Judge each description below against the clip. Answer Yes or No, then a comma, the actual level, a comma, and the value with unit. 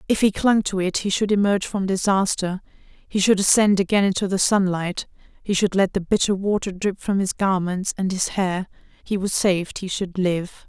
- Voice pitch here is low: No, high, 190 Hz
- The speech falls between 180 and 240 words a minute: Yes, average, 200 wpm